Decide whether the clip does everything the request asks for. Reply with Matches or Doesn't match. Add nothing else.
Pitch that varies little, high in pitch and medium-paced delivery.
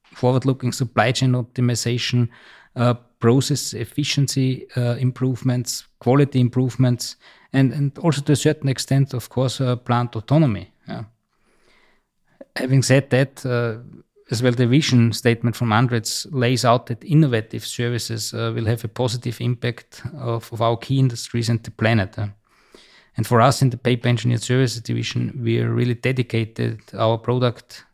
Doesn't match